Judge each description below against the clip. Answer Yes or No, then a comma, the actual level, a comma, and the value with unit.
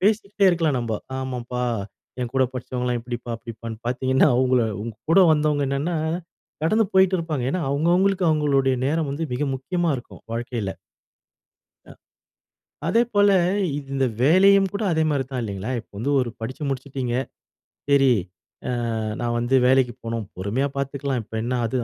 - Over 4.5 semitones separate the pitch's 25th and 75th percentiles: Yes, average, 5.1 semitones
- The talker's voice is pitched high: No, low, 135 Hz